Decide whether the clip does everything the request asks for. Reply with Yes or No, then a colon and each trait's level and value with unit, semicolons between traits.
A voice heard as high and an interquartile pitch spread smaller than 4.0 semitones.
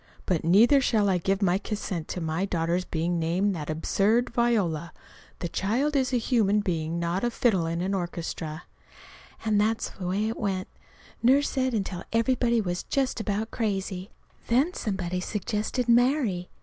No: high, 200 Hz; average, 4.8 semitones